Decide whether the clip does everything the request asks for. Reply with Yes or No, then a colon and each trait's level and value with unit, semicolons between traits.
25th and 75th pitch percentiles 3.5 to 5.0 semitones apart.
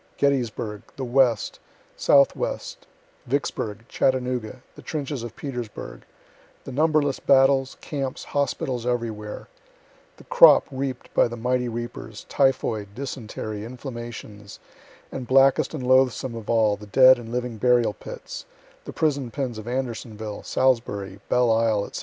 No: average, 3.1 semitones